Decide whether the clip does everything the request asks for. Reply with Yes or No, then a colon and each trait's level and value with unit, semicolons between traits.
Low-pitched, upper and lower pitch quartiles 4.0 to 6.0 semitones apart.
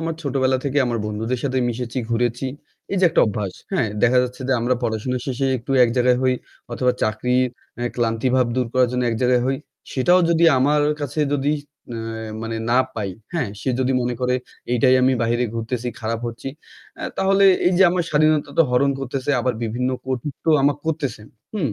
No: low, 125 Hz; average, 2.8 semitones